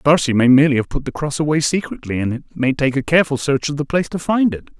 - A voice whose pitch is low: No, medium, 145 Hz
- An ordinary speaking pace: No, fast, 290 wpm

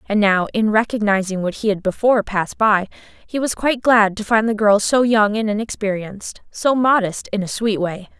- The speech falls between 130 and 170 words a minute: No, average, 200 wpm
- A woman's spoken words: Yes, female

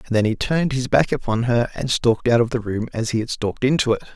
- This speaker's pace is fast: Yes, fast, 290 wpm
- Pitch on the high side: No, low, 120 Hz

